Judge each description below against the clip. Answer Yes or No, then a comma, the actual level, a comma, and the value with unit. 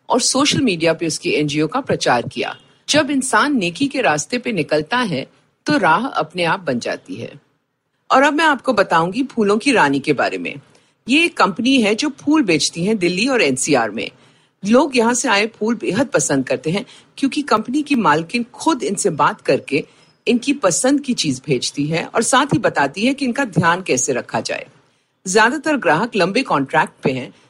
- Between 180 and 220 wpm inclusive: Yes, fast, 190 wpm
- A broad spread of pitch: Yes, wide, 8.6 semitones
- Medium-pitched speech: No, high, 230 Hz